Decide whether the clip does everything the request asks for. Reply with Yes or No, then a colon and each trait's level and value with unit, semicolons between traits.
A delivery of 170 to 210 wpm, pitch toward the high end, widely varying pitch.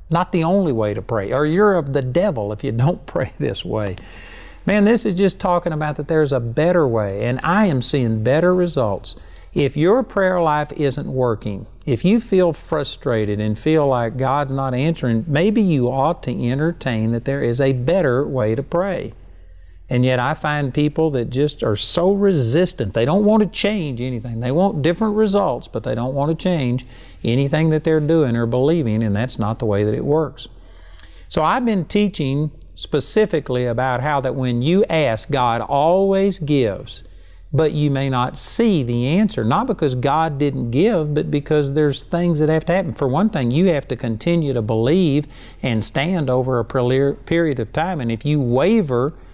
No: average, 190 wpm; medium, 140 Hz; wide, 5.9 semitones